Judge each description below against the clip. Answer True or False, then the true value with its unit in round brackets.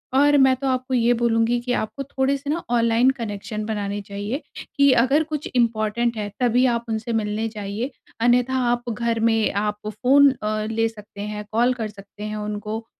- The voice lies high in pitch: True (230 Hz)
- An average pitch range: True (3.1 semitones)